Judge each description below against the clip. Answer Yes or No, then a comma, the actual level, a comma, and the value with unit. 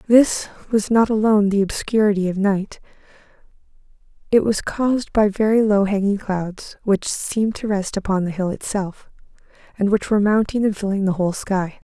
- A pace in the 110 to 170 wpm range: Yes, average, 165 wpm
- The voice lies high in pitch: Yes, high, 205 Hz